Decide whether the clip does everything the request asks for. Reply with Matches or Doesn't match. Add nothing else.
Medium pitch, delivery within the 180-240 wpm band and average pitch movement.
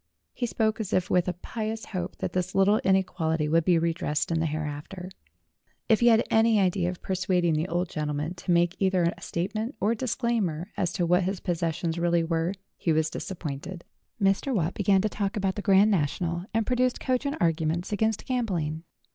Matches